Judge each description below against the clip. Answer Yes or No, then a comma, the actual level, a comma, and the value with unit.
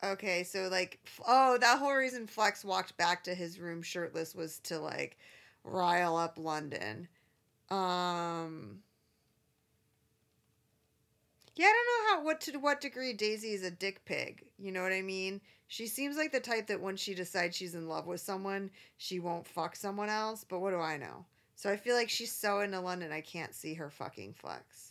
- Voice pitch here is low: No, high, 190 Hz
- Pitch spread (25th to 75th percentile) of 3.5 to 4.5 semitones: Yes, average, 4.2 semitones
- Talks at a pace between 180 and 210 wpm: Yes, average, 190 wpm